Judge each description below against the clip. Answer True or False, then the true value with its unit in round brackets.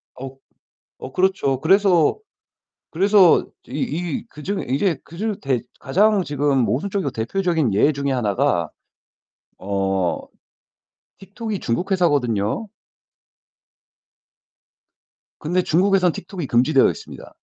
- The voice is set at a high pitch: False (155 Hz)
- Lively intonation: True (6.5 semitones)